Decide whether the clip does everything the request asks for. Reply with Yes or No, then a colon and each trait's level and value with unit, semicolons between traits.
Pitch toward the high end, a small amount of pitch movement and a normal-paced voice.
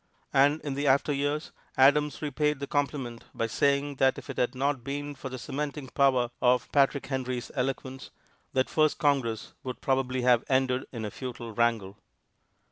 No: low, 135 Hz; narrow, 2.3 semitones; average, 165 wpm